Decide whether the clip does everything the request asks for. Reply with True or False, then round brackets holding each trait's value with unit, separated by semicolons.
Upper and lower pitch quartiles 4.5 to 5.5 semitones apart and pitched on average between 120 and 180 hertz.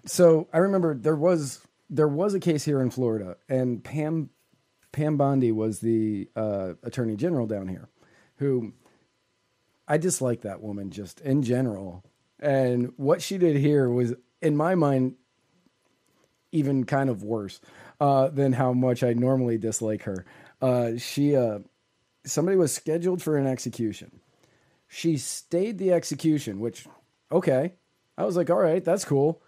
True (4.8 semitones; 135 Hz)